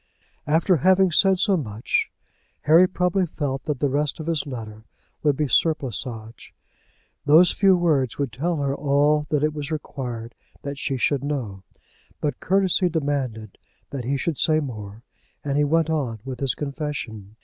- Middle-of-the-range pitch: Yes, medium, 145 Hz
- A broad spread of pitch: No, average, 3.8 semitones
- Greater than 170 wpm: No, average, 160 wpm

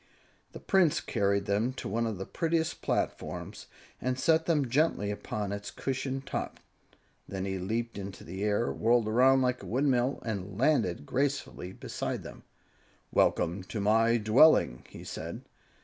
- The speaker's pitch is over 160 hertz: No, low, 115 Hz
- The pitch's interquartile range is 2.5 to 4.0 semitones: No, average, 4.8 semitones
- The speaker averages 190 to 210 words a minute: No, average, 150 wpm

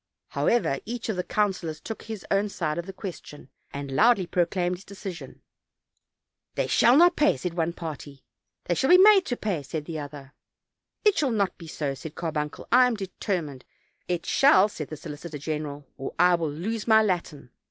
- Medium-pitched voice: Yes, medium, 175 Hz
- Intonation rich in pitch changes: Yes, wide, 5.9 semitones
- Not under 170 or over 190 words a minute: Yes, average, 185 wpm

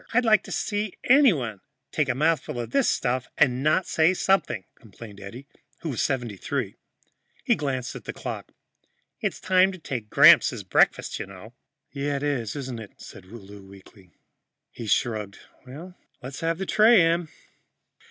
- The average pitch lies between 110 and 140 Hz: Yes, low, 135 Hz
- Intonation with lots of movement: Yes, wide, 7.3 semitones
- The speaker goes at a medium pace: Yes, average, 160 wpm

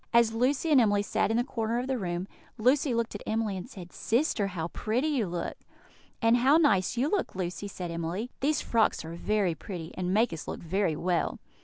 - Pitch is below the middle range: No, high, 215 Hz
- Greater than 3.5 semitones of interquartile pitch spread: Yes, average, 5.1 semitones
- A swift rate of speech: Yes, fast, 210 wpm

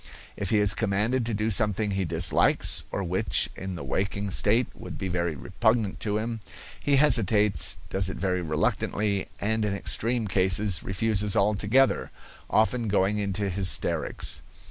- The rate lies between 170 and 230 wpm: No, average, 150 wpm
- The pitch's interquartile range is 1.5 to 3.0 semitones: Yes, narrow, 2.6 semitones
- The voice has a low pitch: Yes, low, 100 Hz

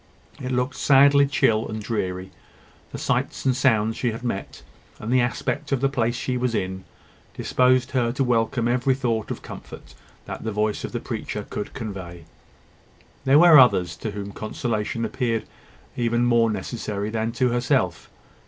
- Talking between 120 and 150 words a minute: No, average, 165 wpm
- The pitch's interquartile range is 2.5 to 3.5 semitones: Yes, average, 3.0 semitones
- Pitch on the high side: No, low, 115 Hz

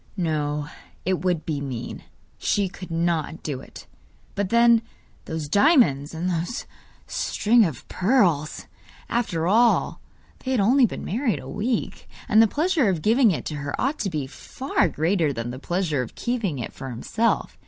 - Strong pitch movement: Yes, wide, 7.4 semitones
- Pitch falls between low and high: Yes, medium, 180 Hz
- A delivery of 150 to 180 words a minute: Yes, average, 165 wpm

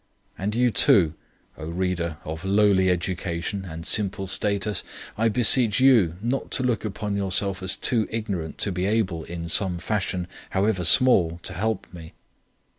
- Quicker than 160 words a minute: No, average, 155 wpm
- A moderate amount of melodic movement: Yes, average, 3.6 semitones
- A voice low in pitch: Yes, very low, 95 Hz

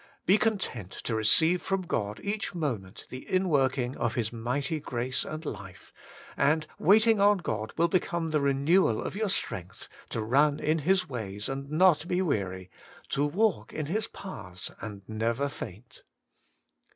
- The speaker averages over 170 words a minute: No, average, 160 wpm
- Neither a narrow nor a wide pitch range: No, wide, 8.0 semitones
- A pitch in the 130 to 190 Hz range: Yes, medium, 140 Hz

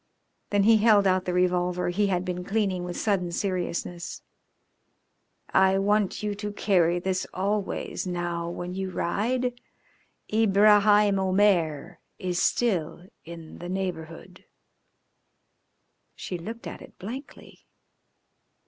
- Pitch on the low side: No, high, 190 Hz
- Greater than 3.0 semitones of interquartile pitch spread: No, average, 2.7 semitones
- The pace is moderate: No, slow, 115 wpm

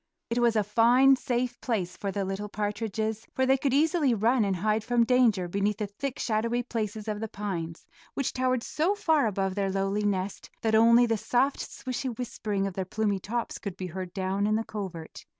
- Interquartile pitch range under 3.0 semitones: No, average, 3.6 semitones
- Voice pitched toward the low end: No, high, 215 Hz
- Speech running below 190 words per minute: No, fast, 205 wpm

